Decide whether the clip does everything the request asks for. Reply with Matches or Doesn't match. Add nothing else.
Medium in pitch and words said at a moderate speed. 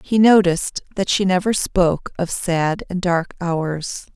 Matches